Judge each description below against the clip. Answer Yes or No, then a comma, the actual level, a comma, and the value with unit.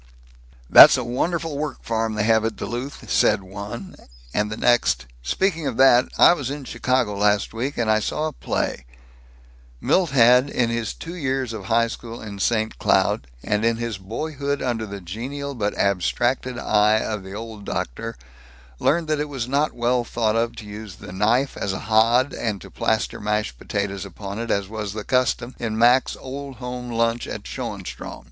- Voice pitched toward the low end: Yes, low, 115 Hz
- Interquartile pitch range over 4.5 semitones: No, average, 3.7 semitones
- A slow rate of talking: No, average, 185 wpm